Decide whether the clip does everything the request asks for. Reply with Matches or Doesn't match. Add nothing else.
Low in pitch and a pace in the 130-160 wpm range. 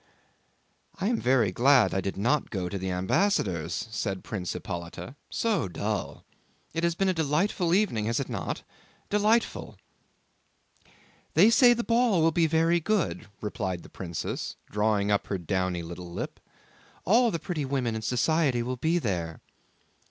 Matches